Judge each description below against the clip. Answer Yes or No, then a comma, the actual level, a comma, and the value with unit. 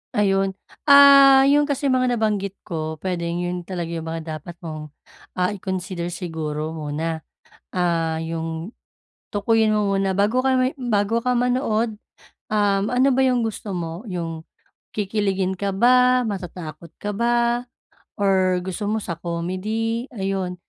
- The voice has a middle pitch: No, high, 195 Hz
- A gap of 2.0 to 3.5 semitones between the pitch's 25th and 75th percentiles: No, average, 5.2 semitones